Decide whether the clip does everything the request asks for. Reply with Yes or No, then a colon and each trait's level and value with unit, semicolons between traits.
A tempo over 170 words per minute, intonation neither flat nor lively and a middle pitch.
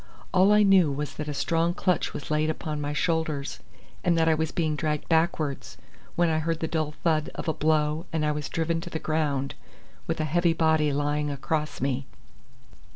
No: average, 200 wpm; narrow, 1.7 semitones; medium, 155 Hz